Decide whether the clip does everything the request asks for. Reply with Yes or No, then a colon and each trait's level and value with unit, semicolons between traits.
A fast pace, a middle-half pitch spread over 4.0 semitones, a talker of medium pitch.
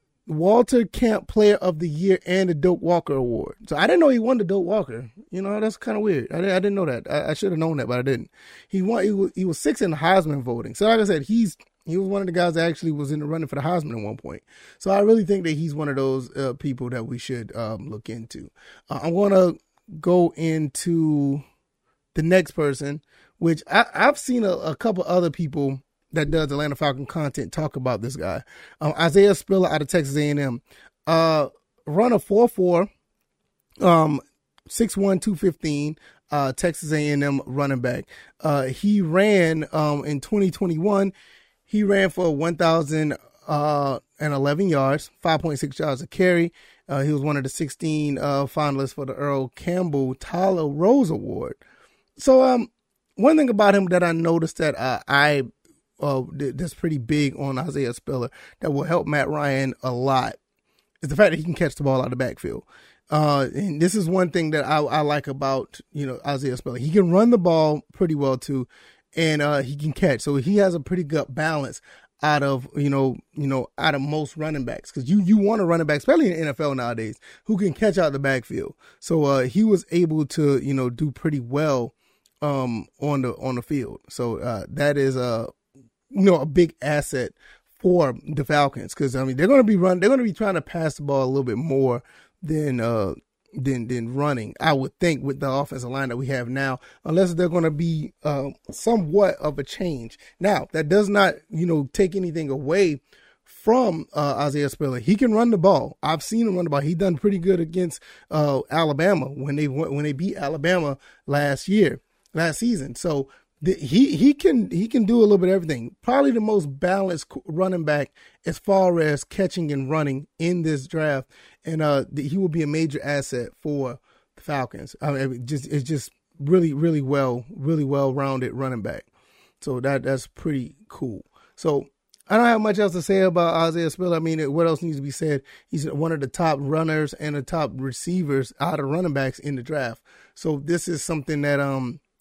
Yes: fast, 210 wpm; average, 4.7 semitones; medium, 155 Hz